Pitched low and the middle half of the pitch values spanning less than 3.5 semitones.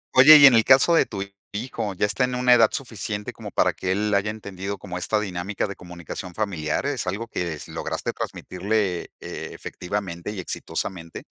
No: low, 105 Hz; average, 4.0 semitones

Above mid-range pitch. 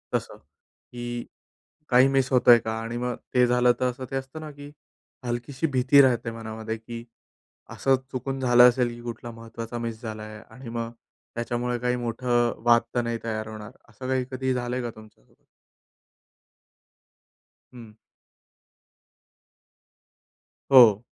No: low, 120 Hz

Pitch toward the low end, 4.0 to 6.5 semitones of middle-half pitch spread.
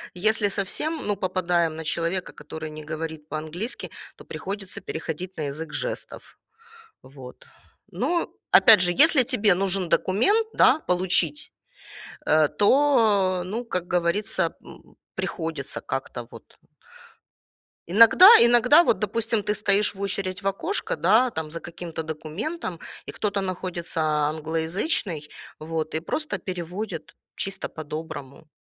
No: medium, 185 Hz; average, 4.7 semitones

